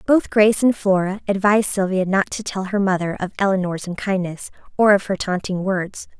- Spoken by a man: No, female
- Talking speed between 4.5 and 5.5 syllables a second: Yes, 5.4 syllables/s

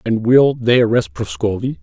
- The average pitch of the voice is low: Yes, low, 110 Hz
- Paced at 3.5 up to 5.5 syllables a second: Yes, 4.7 syllables/s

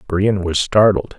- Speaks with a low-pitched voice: Yes, very low, 95 Hz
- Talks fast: No, average, 150 wpm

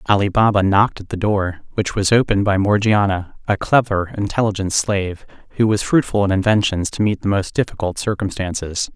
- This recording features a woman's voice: No, male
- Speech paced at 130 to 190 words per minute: Yes, average, 175 wpm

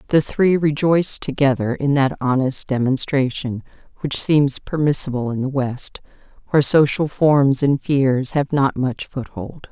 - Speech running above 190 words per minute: No, average, 140 wpm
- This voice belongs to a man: No, female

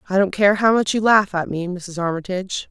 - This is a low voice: No, high, 190 Hz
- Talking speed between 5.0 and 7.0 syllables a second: Yes, 5.6 syllables/s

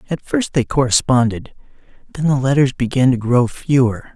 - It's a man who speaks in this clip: Yes, male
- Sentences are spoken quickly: No, average, 160 wpm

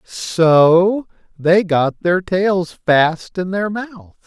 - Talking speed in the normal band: No, slow, 125 wpm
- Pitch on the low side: No, medium, 180 Hz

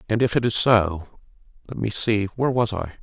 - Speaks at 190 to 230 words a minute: Yes, average, 200 wpm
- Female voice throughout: No, male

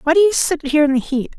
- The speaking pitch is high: Yes, very high, 305 Hz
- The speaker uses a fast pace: Yes, fast, 345 wpm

